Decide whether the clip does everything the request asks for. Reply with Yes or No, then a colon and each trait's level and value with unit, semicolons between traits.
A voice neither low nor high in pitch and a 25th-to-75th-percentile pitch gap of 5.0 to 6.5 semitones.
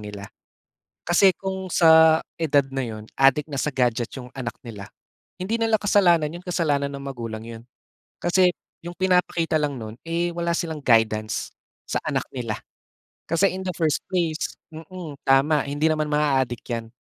Yes: medium, 150 Hz; wide, 5.6 semitones